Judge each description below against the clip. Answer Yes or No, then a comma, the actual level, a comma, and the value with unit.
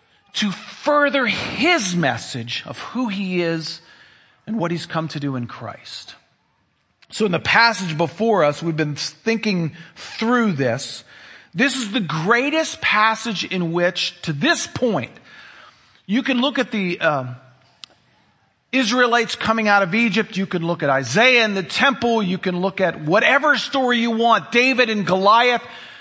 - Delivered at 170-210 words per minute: No, average, 155 wpm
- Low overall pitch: No, high, 205 Hz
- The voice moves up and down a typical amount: No, wide, 5.8 semitones